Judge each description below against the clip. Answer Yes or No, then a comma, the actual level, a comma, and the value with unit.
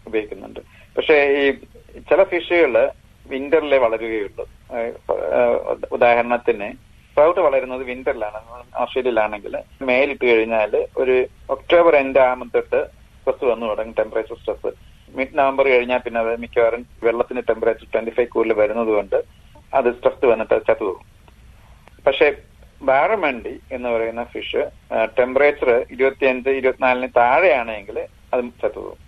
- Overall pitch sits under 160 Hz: Yes, medium, 140 Hz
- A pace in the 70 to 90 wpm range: No, average, 110 wpm